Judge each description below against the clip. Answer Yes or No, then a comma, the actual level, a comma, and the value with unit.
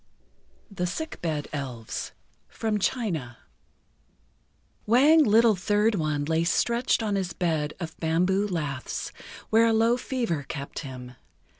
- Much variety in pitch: Yes, wide, 6.7 semitones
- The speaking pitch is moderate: Yes, medium, 180 Hz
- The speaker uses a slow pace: Yes, slow, 125 wpm